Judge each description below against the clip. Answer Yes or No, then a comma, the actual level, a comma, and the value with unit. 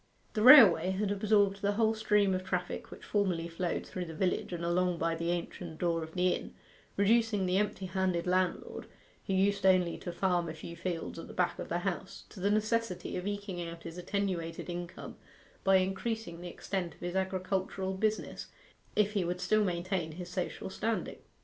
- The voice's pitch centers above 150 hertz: Yes, medium, 185 Hz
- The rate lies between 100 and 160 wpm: No, average, 190 wpm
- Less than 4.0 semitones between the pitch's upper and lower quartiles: Yes, narrow, 2.6 semitones